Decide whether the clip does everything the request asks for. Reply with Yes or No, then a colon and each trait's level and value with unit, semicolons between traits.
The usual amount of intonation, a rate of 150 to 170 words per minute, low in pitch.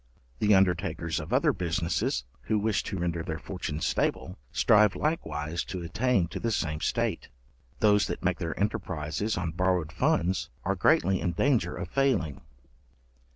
Yes: average, 3.9 semitones; average, 155 wpm; very low, 90 Hz